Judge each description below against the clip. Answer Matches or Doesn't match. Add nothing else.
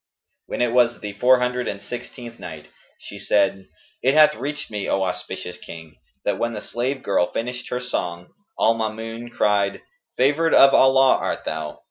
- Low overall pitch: Matches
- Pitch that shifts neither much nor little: Matches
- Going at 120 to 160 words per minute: Doesn't match